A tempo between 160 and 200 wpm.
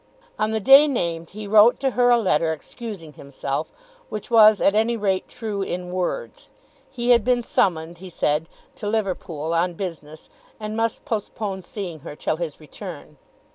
Yes: average, 170 wpm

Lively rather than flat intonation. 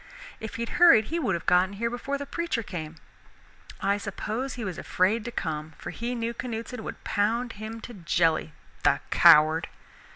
No: average, 4.7 semitones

